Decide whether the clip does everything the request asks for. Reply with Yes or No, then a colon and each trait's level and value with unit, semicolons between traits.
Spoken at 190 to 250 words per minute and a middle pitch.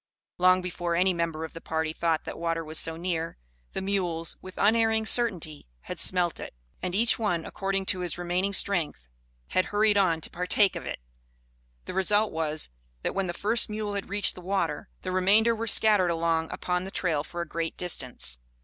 Yes: average, 195 wpm; medium, 180 Hz